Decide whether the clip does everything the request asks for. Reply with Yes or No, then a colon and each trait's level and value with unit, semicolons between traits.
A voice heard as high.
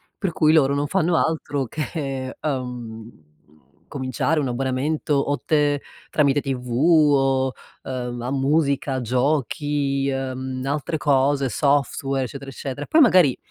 No: medium, 140 Hz